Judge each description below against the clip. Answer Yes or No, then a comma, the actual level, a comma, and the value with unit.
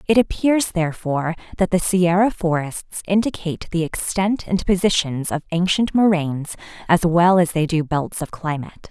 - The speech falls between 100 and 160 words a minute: Yes, average, 155 wpm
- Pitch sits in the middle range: Yes, medium, 175 Hz